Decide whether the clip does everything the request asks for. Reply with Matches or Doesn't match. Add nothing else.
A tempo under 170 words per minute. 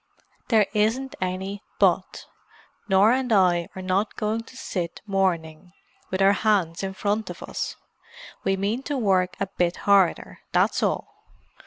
Matches